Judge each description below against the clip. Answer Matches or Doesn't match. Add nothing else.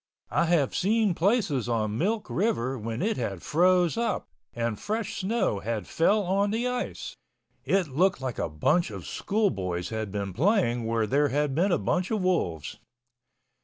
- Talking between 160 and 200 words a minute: Matches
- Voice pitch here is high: Doesn't match